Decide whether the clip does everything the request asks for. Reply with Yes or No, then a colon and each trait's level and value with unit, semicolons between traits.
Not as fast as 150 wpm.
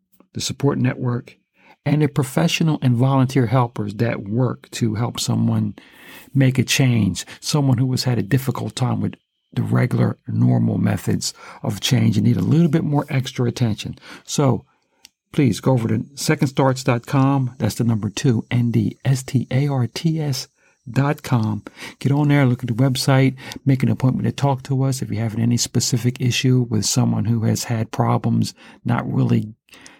No: average, 155 wpm